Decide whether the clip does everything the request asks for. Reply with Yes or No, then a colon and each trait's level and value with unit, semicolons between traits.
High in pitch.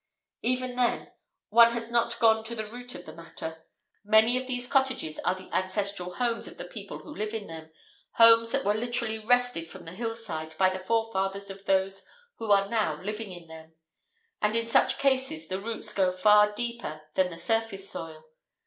Yes: high, 210 Hz